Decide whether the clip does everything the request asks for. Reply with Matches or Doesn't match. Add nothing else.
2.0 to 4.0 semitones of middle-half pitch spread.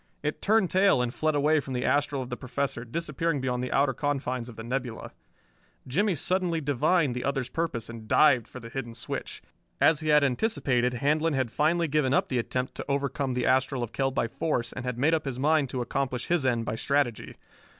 Matches